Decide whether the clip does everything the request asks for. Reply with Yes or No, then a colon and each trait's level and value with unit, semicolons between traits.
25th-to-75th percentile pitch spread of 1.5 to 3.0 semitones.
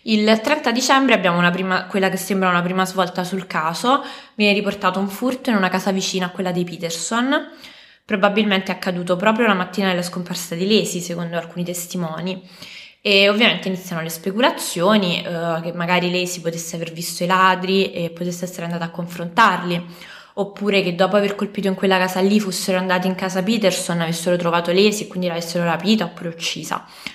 Yes: narrow, 2.5 semitones